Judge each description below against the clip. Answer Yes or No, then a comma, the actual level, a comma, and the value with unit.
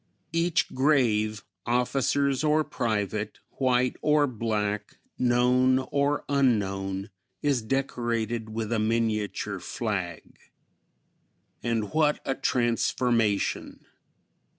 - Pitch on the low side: Yes, low, 120 Hz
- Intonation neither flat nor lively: Yes, average, 3.9 semitones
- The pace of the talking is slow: Yes, slow, 85 wpm